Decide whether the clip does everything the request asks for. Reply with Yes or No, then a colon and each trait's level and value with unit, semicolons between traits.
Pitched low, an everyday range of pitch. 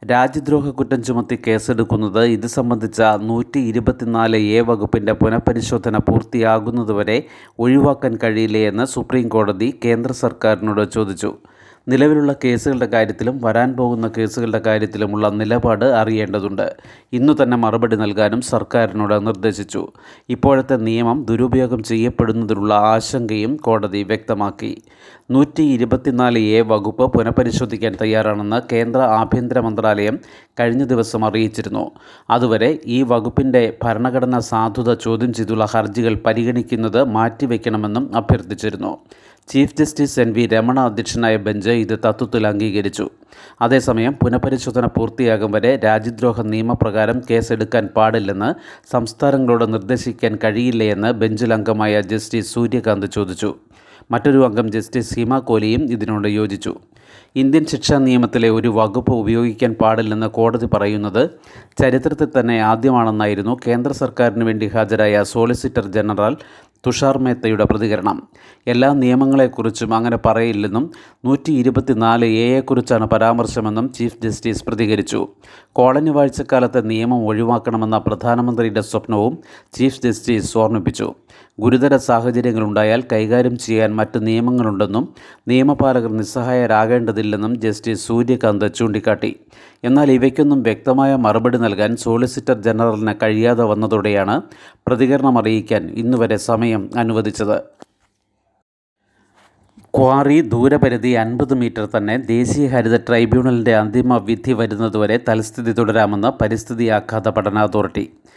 No: low, 115 Hz; narrow, 2.3 semitones